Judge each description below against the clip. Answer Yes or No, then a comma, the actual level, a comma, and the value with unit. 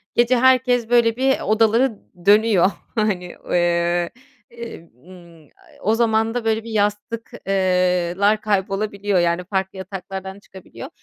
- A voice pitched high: Yes, high, 205 Hz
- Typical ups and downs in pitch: Yes, average, 3.4 semitones